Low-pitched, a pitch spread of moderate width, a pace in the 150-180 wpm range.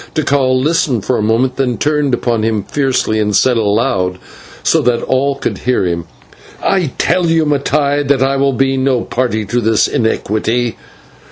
Yes: low, 130 Hz; average, 3.8 semitones; average, 170 wpm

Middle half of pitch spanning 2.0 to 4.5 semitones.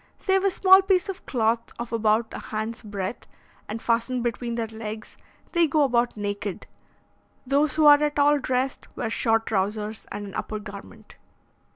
No: average, 5.1 semitones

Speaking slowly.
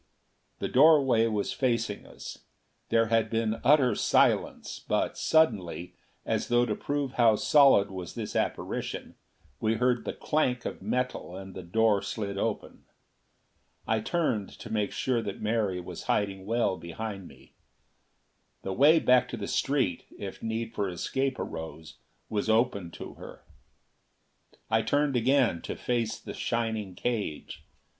No: average, 145 wpm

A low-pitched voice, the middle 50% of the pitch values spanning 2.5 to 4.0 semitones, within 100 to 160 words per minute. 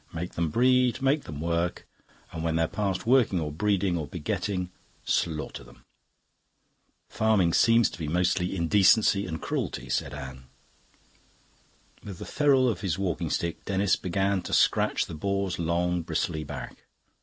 Yes: very low, 90 Hz; average, 3.7 semitones; average, 150 wpm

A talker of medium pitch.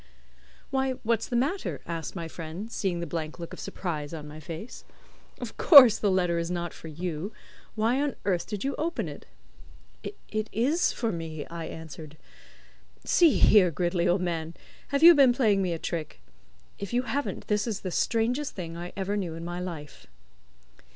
Yes: medium, 180 Hz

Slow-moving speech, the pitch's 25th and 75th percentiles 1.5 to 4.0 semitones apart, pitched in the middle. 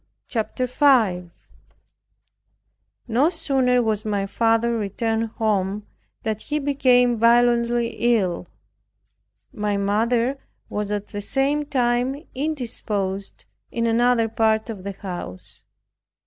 No: slow, 105 wpm; average, 3.2 semitones; high, 230 Hz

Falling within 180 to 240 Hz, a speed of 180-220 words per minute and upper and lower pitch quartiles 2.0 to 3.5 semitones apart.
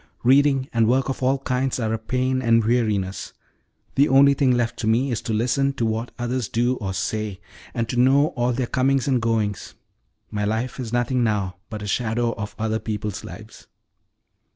No: low, 120 Hz; average, 190 wpm; average, 2.8 semitones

